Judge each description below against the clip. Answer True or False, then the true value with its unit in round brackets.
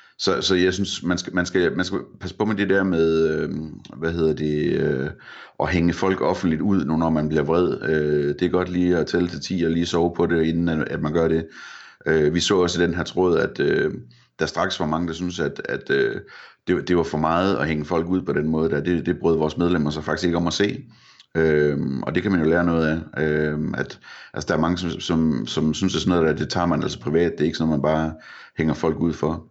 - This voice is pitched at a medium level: False (80 Hz)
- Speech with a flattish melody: True (2.2 semitones)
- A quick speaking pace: True (275 wpm)